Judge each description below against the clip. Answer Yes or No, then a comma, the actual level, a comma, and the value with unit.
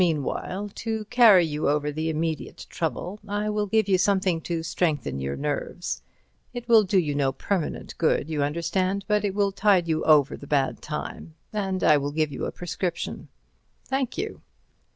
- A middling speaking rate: Yes, average, 175 wpm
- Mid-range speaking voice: Yes, medium, 175 Hz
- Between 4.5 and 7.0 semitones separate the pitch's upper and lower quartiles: Yes, average, 5.2 semitones